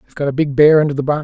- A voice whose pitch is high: No, medium, 145 Hz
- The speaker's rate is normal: No, fast, 390 wpm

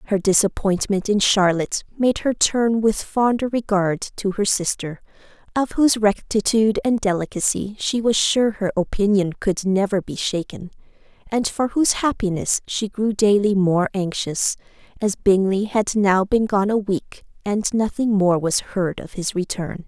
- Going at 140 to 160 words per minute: Yes, average, 155 wpm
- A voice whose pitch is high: Yes, high, 205 Hz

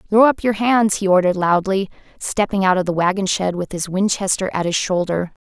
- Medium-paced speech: No, fast, 210 wpm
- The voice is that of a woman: Yes, female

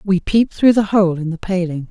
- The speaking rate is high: Yes, fast, 250 wpm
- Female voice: Yes, female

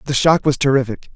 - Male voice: Yes, male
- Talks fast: Yes, fast, 210 wpm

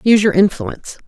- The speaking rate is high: No, average, 170 wpm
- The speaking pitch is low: No, high, 205 Hz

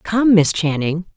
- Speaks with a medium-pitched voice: Yes, medium, 180 Hz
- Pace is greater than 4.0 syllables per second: No, 3.8 syllables/s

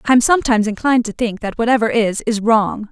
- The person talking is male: No, female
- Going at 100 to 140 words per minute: No, fast, 205 wpm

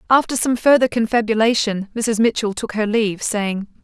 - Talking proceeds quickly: No, average, 155 wpm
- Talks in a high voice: Yes, high, 220 Hz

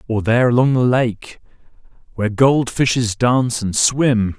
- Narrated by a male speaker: Yes, male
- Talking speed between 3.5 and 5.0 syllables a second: Yes, 4.6 syllables/s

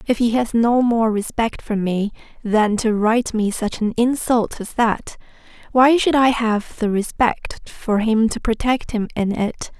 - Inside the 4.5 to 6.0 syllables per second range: No, 4.1 syllables/s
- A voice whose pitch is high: Yes, high, 225 Hz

